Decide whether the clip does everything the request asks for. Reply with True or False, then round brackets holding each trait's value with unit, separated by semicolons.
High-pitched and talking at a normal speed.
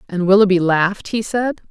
True (195 Hz; 175 wpm)